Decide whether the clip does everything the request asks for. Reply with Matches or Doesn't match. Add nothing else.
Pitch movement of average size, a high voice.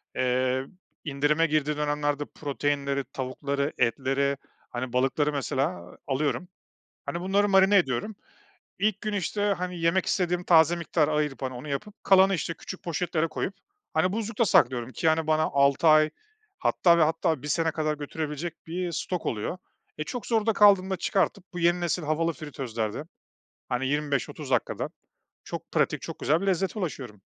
Doesn't match